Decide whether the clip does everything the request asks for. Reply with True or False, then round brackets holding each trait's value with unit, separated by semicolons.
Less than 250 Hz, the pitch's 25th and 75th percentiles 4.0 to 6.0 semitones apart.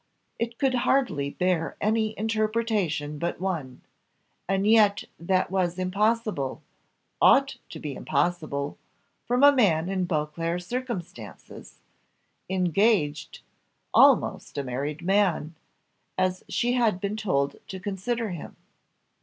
True (185 Hz; 5.6 semitones)